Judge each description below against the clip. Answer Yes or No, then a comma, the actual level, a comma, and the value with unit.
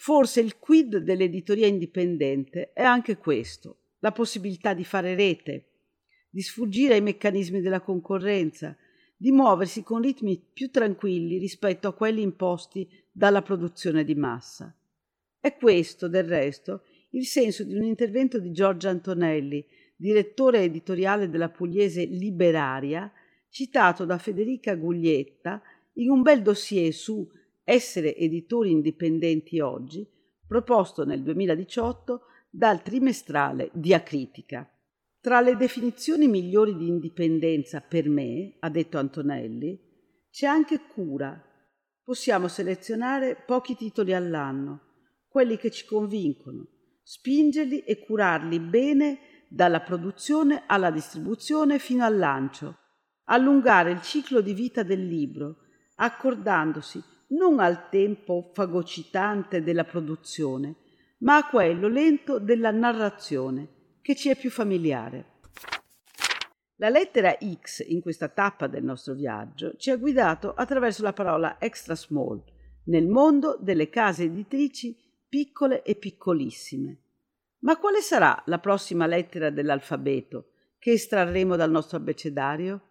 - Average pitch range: No, wide, 6.5 semitones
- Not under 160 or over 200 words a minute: No, average, 120 wpm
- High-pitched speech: Yes, high, 195 Hz